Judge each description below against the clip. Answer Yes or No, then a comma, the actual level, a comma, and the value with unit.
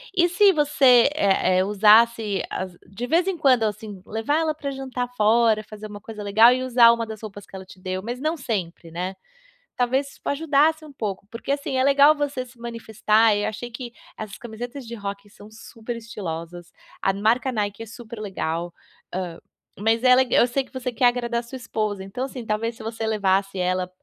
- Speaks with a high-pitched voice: Yes, high, 225 Hz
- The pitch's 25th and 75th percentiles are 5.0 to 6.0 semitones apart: No, average, 3.9 semitones